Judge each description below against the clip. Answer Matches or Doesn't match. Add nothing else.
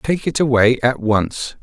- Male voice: Matches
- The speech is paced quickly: Doesn't match